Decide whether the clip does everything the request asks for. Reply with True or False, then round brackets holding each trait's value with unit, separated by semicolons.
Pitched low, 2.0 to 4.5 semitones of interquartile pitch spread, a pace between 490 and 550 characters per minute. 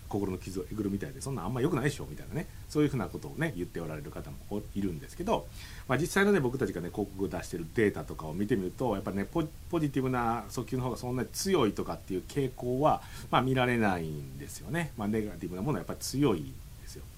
False (105 Hz; 5.5 semitones; 515 characters per minute)